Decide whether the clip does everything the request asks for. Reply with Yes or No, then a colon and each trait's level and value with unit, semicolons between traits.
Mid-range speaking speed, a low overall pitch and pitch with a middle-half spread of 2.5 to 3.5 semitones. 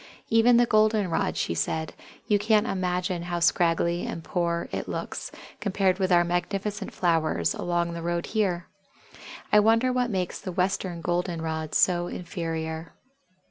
No: average, 150 wpm; medium, 175 Hz; average, 3.1 semitones